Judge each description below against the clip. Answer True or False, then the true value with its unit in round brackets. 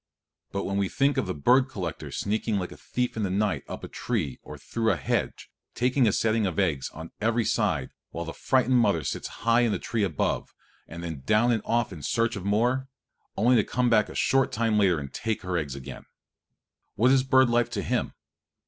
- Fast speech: True (220 wpm)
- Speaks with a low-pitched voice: True (110 Hz)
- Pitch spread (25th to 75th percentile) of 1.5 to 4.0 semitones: False (4.6 semitones)